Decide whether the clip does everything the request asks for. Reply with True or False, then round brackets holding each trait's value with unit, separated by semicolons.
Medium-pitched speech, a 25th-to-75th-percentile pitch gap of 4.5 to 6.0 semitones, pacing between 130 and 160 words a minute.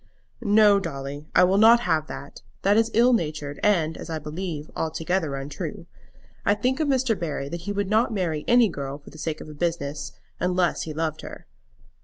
False (165 Hz; 5.2 semitones; 195 wpm)